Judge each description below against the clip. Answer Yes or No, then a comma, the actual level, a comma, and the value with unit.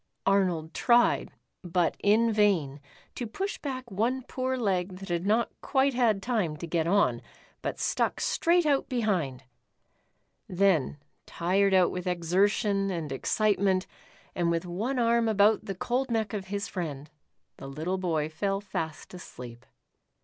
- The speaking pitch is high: Yes, high, 195 Hz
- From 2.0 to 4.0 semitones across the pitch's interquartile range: No, average, 4.7 semitones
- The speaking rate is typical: Yes, average, 150 wpm